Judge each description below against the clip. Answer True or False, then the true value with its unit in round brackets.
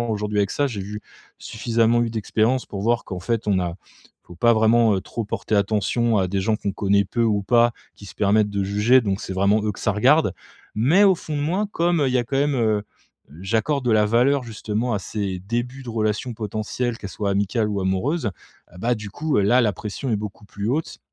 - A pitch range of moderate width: True (3.1 semitones)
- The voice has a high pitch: False (110 Hz)